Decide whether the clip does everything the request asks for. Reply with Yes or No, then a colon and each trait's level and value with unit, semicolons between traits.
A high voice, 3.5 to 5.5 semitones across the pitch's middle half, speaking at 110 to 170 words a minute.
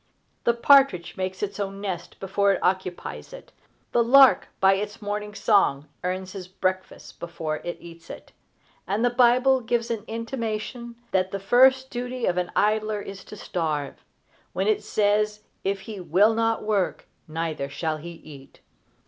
Yes: high, 205 Hz; average, 4.0 semitones; average, 160 wpm